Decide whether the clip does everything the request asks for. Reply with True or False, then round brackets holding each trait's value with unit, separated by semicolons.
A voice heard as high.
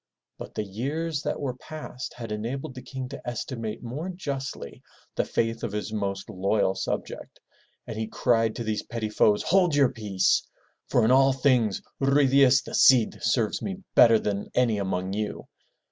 False (120 Hz)